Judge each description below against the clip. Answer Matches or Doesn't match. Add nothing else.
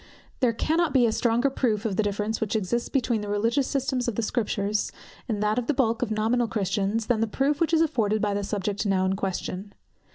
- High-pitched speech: Matches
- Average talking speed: Doesn't match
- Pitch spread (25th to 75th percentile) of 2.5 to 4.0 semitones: Matches